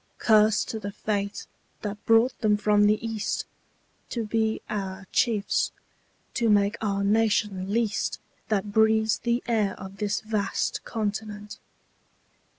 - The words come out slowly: Yes, slow, 130 wpm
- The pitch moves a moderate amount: No, narrow, 1.5 semitones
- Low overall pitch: No, high, 210 Hz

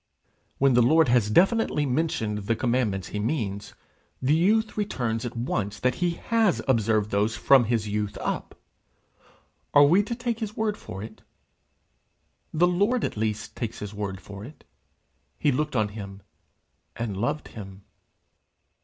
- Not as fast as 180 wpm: Yes, average, 155 wpm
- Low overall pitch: Yes, low, 120 Hz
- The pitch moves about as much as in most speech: No, wide, 7.4 semitones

